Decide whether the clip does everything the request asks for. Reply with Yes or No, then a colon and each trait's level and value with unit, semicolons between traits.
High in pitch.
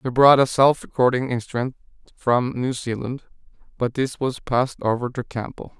No: low, 125 Hz